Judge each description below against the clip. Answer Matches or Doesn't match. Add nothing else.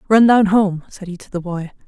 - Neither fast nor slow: Doesn't match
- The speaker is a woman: Matches